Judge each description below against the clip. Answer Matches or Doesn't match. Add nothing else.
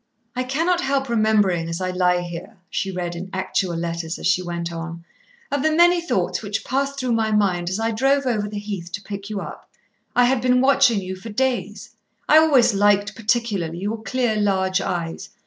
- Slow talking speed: Doesn't match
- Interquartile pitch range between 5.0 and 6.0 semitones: Matches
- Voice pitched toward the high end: Matches